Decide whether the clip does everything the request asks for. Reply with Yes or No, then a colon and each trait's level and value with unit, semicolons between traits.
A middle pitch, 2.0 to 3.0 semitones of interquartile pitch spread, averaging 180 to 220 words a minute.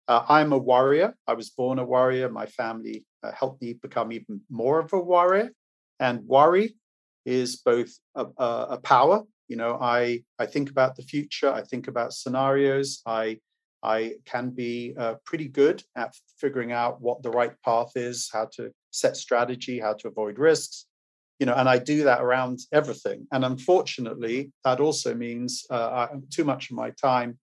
No: low, 125 Hz; narrow, 2.5 semitones; average, 185 wpm